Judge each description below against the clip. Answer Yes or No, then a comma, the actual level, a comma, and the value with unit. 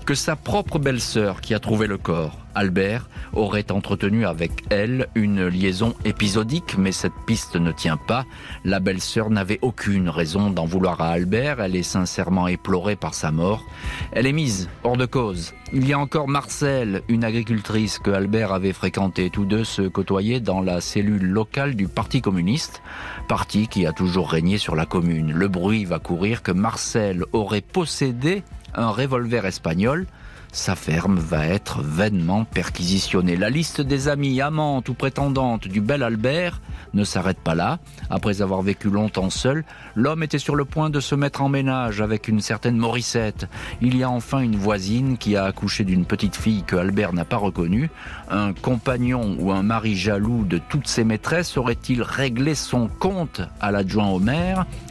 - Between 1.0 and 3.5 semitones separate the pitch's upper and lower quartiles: No, average, 4.8 semitones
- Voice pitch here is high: No, low, 105 Hz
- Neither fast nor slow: Yes, average, 175 wpm